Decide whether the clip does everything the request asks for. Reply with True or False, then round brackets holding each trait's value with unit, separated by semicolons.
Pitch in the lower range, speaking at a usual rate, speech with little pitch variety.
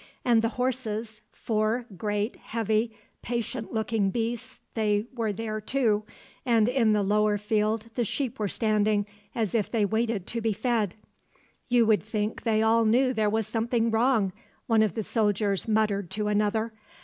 False (220 Hz; 160 wpm; 1.6 semitones)